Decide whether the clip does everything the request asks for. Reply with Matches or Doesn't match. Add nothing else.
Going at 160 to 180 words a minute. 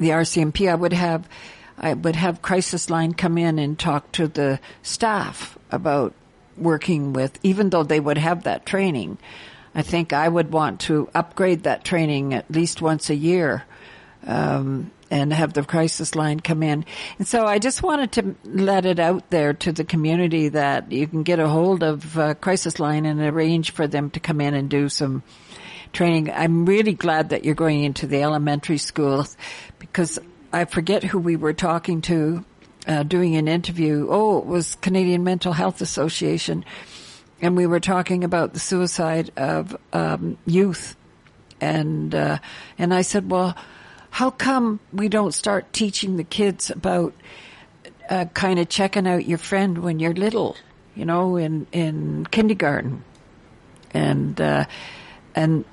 Matches